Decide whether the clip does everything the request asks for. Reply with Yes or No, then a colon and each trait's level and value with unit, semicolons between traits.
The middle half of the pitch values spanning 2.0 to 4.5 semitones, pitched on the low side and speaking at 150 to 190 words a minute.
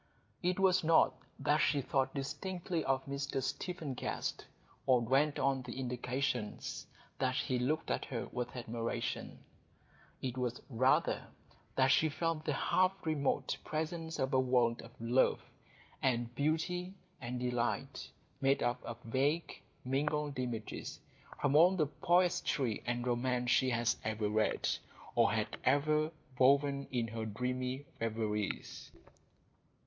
No: average, 3.8 semitones; low, 130 Hz; slow, 135 wpm